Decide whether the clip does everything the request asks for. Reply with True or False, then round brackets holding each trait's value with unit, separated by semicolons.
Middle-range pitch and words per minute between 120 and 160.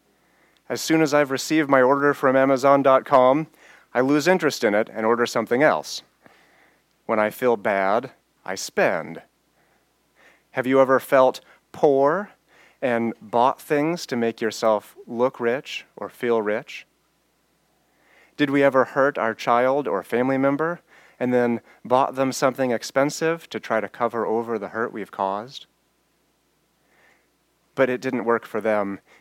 False (130 Hz; 145 wpm)